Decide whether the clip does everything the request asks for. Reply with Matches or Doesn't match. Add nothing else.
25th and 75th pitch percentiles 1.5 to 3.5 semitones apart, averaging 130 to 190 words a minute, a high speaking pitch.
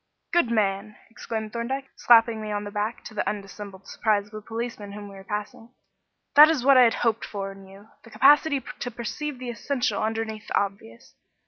Doesn't match